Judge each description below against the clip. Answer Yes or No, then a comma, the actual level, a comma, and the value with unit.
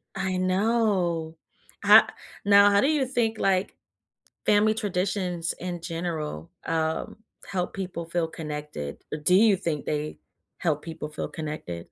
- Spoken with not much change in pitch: No, average, 4.0 semitones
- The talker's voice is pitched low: No, medium, 175 Hz